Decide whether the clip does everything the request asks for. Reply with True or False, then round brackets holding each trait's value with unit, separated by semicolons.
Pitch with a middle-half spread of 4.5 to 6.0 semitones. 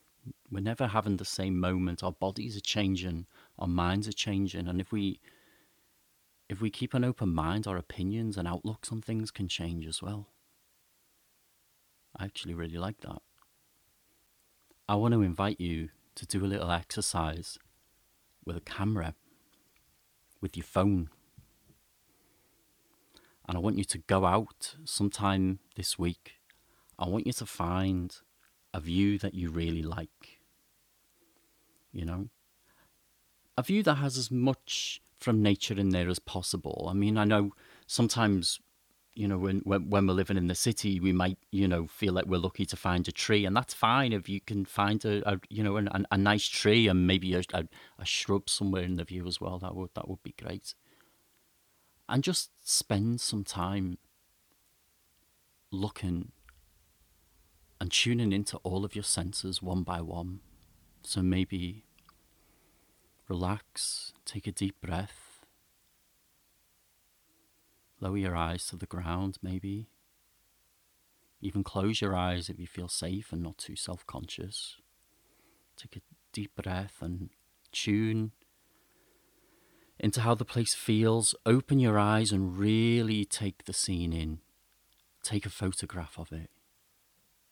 False (2.8 semitones)